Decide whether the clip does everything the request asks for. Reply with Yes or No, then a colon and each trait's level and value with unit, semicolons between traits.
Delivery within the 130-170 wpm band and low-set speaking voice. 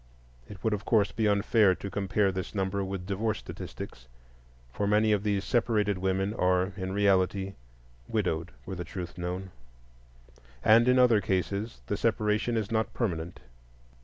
Yes: average, 155 wpm; low, 100 Hz